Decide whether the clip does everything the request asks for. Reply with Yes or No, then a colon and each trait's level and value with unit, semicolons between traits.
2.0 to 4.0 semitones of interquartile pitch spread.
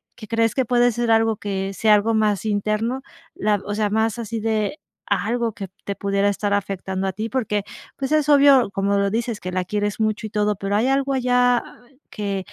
Yes: average, 2.8 semitones